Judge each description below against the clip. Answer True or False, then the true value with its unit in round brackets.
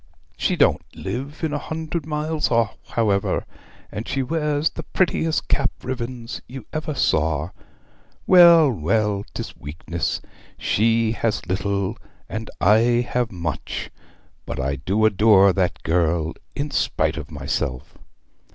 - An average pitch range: False (8.0 semitones)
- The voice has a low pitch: True (115 Hz)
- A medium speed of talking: False (125 wpm)